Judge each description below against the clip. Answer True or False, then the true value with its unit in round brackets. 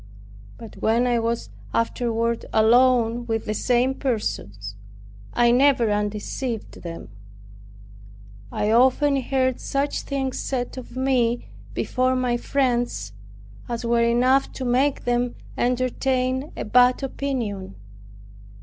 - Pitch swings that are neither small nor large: False (2.1 semitones)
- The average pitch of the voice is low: False (245 Hz)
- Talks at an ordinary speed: False (115 wpm)